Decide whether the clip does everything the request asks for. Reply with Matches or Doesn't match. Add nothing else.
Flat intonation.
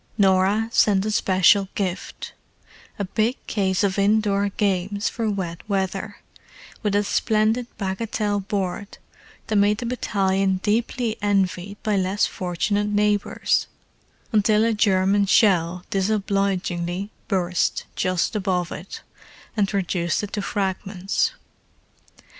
Matches